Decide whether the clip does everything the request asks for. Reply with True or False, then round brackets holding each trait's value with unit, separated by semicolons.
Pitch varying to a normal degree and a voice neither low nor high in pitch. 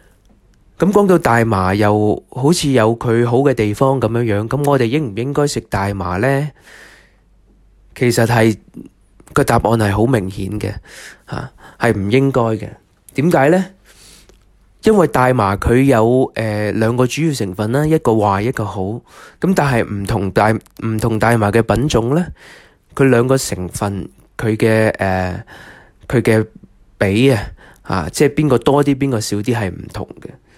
False (4.4 semitones; 115 Hz)